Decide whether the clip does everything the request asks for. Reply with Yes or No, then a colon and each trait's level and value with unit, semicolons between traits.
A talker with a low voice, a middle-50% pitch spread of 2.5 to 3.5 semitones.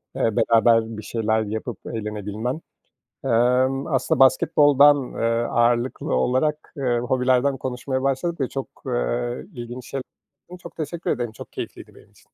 Yes: low, 125 Hz; average, 2.8 semitones